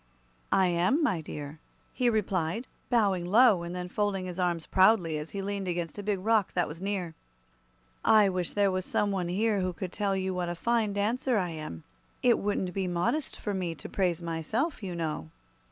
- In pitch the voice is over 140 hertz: Yes, medium, 185 Hz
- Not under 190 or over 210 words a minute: Yes, average, 200 wpm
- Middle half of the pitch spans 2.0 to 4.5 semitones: Yes, average, 3.1 semitones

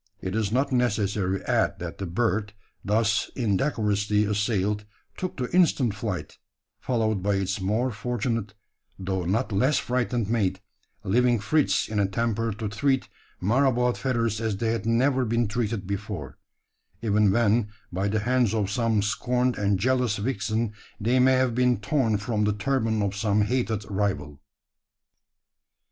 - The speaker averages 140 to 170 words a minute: Yes, average, 150 wpm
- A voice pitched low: Yes, low, 110 Hz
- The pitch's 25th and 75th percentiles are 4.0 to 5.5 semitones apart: No, average, 3.4 semitones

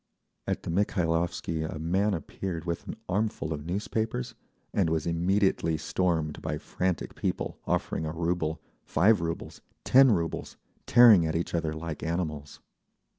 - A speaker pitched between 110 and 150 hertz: No, very low, 85 Hz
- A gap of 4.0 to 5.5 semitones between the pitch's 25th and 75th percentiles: No, average, 3.0 semitones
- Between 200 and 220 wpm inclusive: No, average, 140 wpm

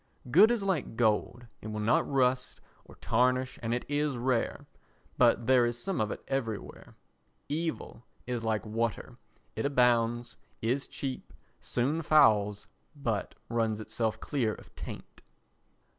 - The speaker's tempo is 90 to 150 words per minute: Yes, average, 140 wpm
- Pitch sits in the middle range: No, low, 120 Hz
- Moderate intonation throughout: Yes, average, 3.3 semitones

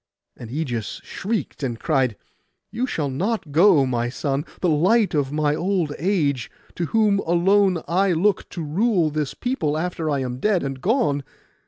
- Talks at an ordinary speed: Yes, average, 165 wpm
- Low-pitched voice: No, medium, 160 Hz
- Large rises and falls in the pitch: Yes, wide, 5.8 semitones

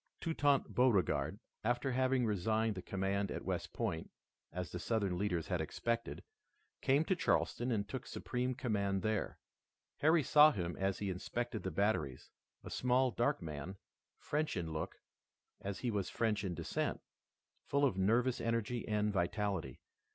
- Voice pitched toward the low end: Yes, low, 110 Hz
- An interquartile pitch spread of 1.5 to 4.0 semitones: No, average, 4.5 semitones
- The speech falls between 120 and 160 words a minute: Yes, average, 150 wpm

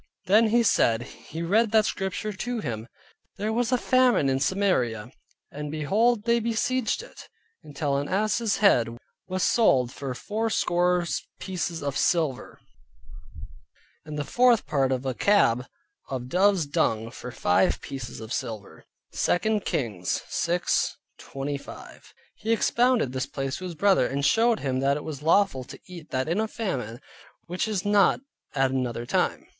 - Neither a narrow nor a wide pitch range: No, wide, 8.3 semitones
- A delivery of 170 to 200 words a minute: No, average, 155 wpm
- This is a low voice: No, medium, 170 Hz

